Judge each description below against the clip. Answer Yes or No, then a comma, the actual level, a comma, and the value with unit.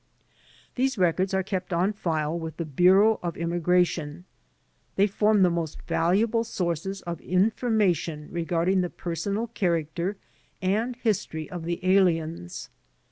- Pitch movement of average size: Yes, average, 3.0 semitones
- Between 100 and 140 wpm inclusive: Yes, slow, 135 wpm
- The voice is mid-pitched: Yes, medium, 180 Hz